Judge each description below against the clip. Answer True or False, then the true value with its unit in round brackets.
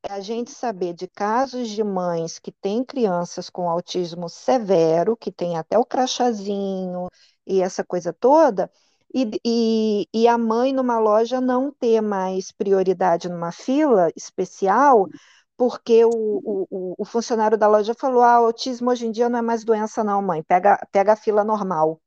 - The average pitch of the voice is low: False (215 Hz)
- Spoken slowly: False (165 wpm)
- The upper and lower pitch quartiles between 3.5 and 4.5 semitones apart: True (4.2 semitones)